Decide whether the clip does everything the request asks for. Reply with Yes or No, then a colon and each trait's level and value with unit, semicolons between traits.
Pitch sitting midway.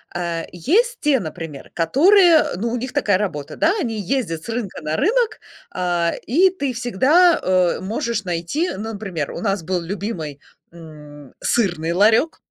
No: high, 200 Hz